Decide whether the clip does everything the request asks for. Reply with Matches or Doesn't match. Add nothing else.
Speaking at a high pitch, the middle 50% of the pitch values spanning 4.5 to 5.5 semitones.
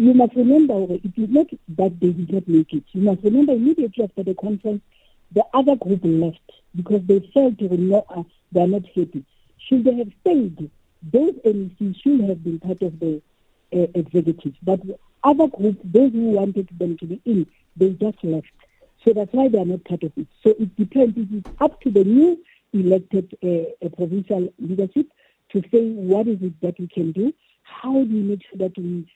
Matches